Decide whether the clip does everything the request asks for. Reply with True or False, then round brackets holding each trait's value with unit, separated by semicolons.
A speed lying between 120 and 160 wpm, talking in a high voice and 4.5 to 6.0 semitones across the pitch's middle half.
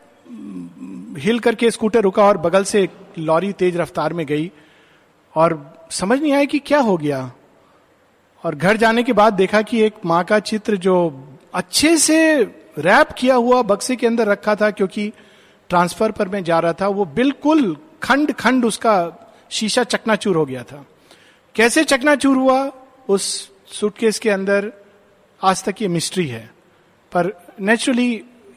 True (155 wpm; 205 Hz; 5.0 semitones)